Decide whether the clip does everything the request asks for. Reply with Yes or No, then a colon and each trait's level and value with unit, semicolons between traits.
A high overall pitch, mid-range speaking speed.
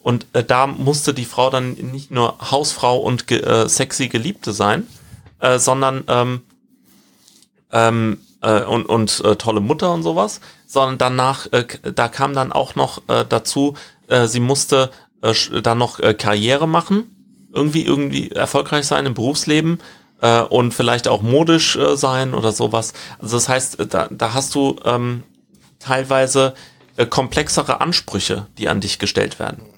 No: low, 130 Hz; average, 160 wpm